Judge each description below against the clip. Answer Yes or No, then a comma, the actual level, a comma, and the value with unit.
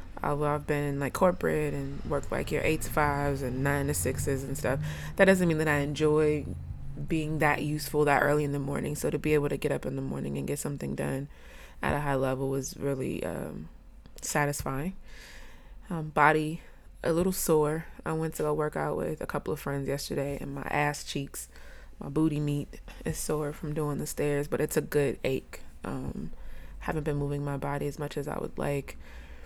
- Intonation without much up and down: Yes, narrow, 1.6 semitones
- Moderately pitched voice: Yes, medium, 145 Hz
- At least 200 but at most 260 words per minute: Yes, fast, 205 wpm